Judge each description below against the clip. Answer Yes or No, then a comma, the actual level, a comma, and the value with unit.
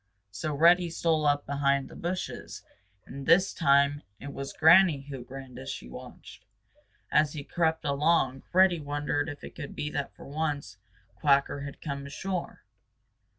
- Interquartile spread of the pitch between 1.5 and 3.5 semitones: Yes, narrow, 2.6 semitones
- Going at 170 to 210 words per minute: No, average, 155 wpm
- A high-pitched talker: No, medium, 145 Hz